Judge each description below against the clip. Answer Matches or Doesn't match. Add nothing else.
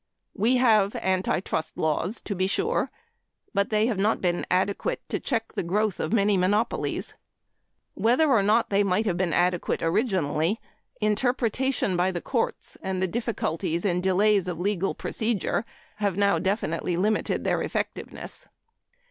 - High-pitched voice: Matches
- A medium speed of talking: Matches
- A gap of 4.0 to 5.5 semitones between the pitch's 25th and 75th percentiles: Doesn't match